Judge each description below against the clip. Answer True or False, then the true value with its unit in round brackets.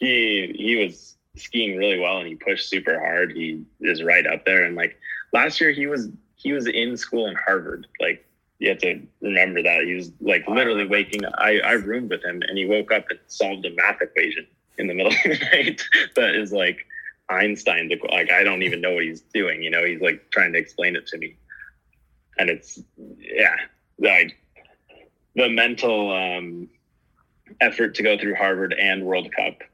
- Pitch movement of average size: False (5.9 semitones)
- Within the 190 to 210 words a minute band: True (195 wpm)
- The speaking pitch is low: True (105 Hz)